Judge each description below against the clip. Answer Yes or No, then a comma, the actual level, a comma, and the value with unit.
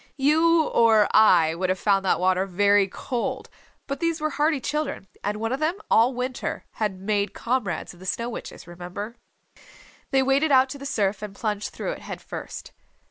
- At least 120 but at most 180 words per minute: No, average, 190 wpm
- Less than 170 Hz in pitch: No, high, 225 Hz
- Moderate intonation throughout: No, wide, 5.9 semitones